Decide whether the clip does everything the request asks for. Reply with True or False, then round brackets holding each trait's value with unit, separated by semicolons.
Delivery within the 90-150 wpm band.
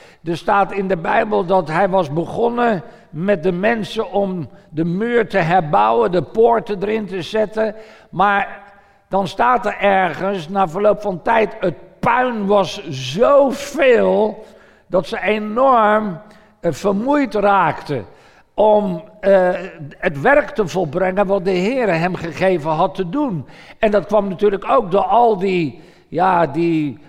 True (140 wpm)